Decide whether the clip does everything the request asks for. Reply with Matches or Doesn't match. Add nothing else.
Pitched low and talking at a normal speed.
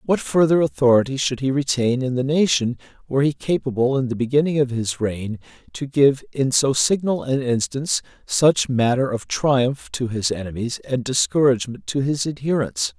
Matches